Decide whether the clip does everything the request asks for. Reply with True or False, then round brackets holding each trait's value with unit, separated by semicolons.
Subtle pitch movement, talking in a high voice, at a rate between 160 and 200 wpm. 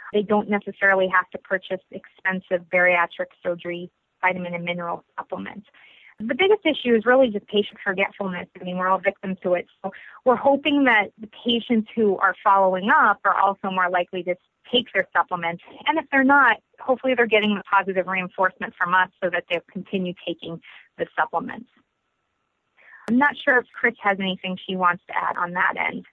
False (4.4 semitones; 195 Hz; 180 wpm)